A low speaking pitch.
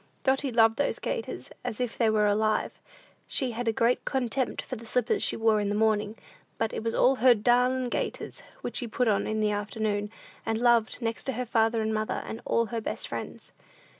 No: high, 225 Hz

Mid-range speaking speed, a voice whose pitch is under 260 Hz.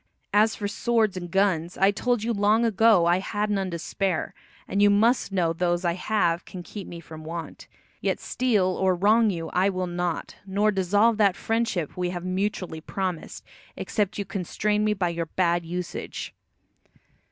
Yes: average, 175 wpm; high, 190 Hz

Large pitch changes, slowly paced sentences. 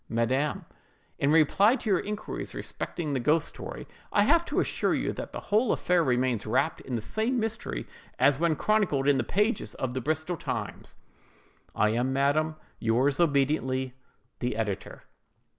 No: wide, 5.9 semitones; average, 160 wpm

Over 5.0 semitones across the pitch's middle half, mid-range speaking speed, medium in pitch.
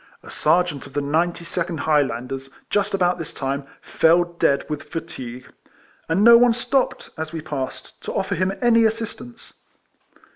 Yes: wide, 5.6 semitones; average, 155 wpm; medium, 170 Hz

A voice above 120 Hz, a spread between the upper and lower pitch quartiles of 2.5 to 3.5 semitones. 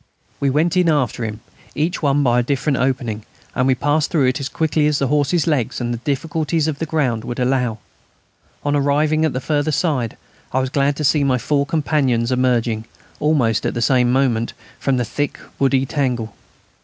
Yes: low, 135 Hz; average, 3.2 semitones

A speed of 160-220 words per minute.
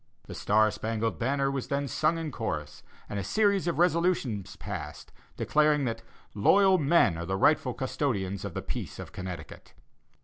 Yes: average, 165 wpm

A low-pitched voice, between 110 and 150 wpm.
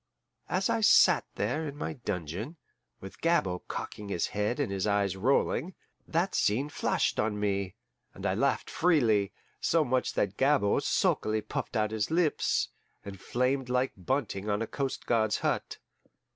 No: low, 110 Hz; average, 160 wpm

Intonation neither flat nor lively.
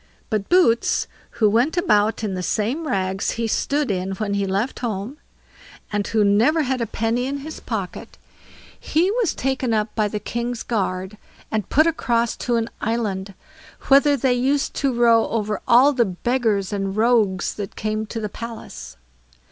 Yes: average, 3.9 semitones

